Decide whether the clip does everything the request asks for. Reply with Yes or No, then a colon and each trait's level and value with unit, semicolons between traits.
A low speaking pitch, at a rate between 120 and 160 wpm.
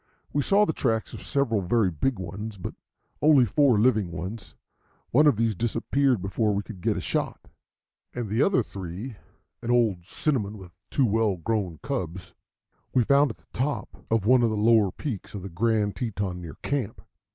No: low, 110 Hz; average, 185 wpm